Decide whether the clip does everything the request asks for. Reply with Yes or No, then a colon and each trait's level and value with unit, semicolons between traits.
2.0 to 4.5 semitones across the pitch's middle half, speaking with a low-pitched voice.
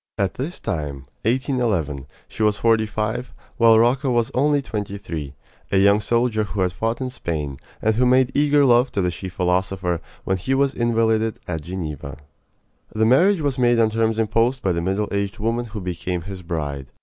No: average, 4.9 semitones; low, 110 Hz